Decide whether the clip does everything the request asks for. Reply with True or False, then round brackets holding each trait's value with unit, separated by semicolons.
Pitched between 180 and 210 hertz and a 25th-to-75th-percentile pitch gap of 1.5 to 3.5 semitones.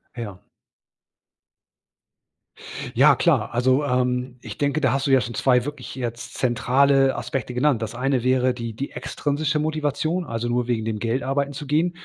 False (130 Hz; 2.9 semitones)